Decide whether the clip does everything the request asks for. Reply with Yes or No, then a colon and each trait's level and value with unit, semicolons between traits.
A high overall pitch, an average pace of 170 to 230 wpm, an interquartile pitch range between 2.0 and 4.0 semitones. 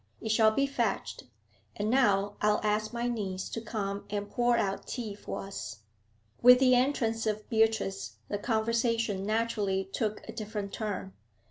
No: high, 215 Hz; average, 155 wpm; narrow, 2.4 semitones